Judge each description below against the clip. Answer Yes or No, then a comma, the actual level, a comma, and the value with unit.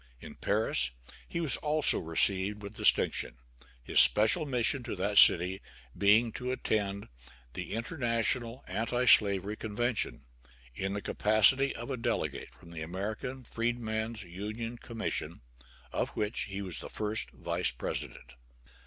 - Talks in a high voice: No, low, 110 Hz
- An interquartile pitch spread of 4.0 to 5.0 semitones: No, average, 3.3 semitones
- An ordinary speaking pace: No, slow, 130 wpm